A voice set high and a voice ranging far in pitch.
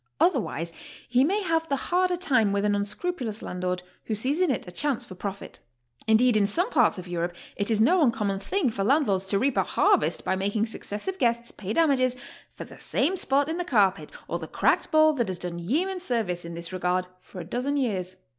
Yes: high, 225 Hz; wide, 7.1 semitones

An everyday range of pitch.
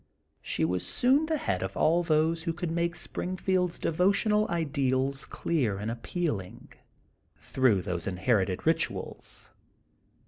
No: wide, 8.7 semitones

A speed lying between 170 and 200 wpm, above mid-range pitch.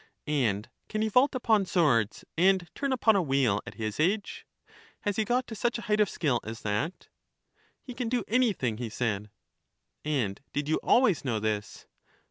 No: average, 180 wpm; medium, 165 Hz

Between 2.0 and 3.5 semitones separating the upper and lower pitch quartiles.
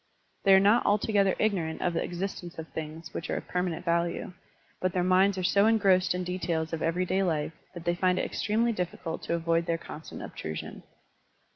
Yes: narrow, 2.5 semitones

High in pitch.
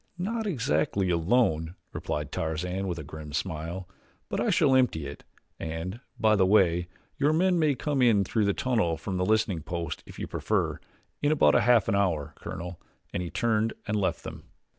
No: very low, 95 Hz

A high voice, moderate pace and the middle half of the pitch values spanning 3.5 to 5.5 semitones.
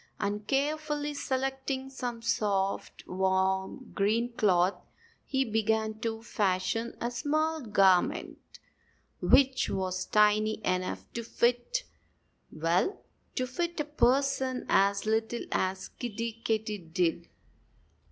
No: high, 225 Hz; slow, 105 wpm; average, 5.1 semitones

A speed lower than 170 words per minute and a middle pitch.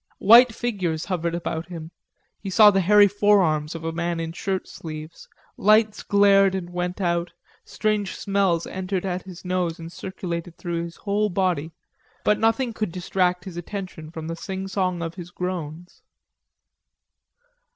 Yes: average, 150 wpm; medium, 180 Hz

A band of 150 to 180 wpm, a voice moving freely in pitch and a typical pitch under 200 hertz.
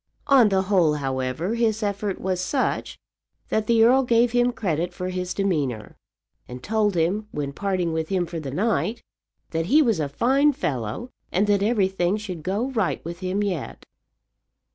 No: average, 170 wpm; average, 4.9 semitones; high, 190 Hz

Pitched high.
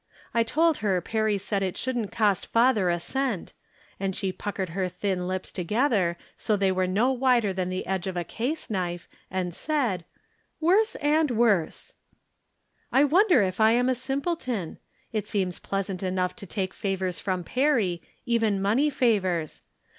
Yes: high, 205 Hz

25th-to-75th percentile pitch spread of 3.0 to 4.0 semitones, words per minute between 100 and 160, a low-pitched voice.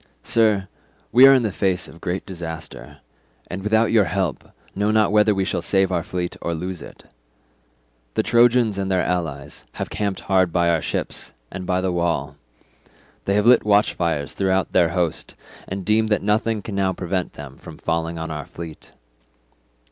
No: average, 3.6 semitones; average, 180 wpm; very low, 95 Hz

